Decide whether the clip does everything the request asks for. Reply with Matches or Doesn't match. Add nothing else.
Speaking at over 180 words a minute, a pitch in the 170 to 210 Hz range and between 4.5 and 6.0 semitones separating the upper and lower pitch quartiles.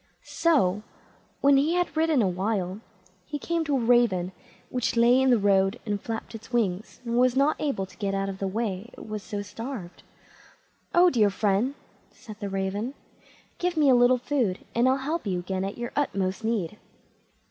Doesn't match